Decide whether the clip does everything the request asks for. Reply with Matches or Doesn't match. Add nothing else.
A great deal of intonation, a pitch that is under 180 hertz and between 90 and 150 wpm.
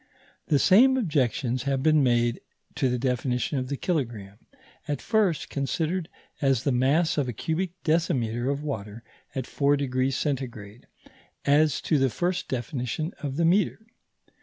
Doesn't match